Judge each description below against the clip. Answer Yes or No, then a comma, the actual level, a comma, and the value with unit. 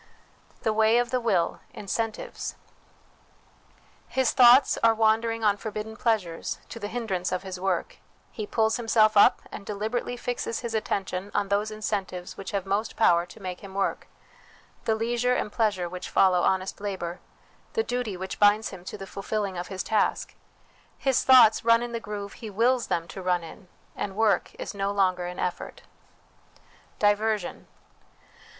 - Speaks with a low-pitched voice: No, high, 210 Hz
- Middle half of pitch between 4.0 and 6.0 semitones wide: No, average, 3.0 semitones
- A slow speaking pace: No, average, 165 wpm